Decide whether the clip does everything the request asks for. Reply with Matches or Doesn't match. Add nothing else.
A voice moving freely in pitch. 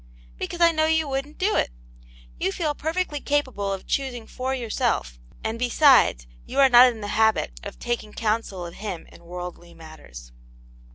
Matches